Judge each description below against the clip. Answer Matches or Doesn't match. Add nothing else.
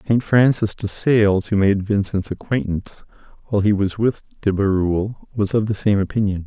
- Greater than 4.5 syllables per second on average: Matches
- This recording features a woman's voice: Doesn't match